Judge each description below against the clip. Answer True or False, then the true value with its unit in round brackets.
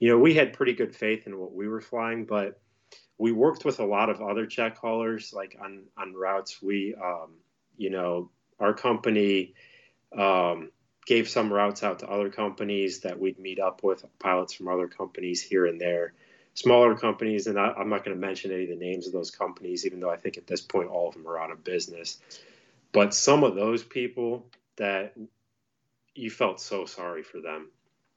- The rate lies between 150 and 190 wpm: False (200 wpm)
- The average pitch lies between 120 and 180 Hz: False (105 Hz)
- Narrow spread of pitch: False (3.2 semitones)